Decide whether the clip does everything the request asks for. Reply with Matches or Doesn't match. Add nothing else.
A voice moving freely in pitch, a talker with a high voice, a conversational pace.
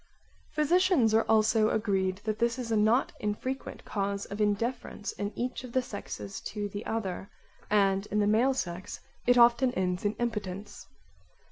Doesn't match